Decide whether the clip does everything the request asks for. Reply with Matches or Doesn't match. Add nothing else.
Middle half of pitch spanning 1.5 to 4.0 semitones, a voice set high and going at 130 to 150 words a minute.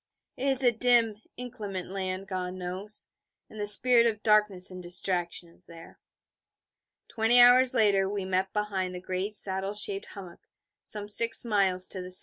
Doesn't match